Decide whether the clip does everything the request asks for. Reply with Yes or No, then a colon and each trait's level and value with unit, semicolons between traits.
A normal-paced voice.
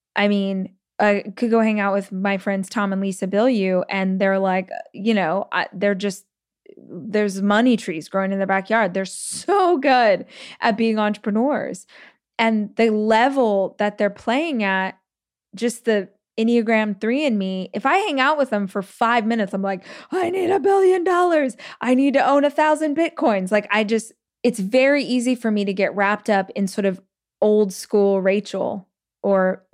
Yes: average, 185 wpm